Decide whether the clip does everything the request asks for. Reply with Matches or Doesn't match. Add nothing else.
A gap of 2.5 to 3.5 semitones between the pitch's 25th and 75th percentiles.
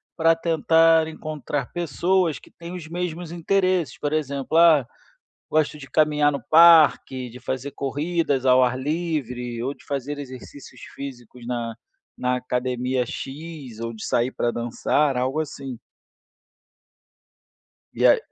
Doesn't match